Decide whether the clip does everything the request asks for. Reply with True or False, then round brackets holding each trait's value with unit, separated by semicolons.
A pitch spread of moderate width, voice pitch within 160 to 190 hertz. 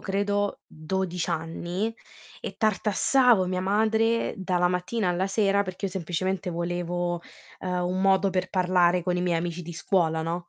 False (2.0 semitones; 185 Hz)